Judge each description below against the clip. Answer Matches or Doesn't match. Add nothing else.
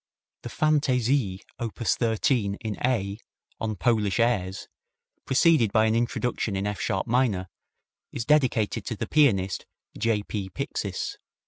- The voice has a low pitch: Matches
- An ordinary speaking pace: Doesn't match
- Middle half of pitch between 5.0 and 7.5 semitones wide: Doesn't match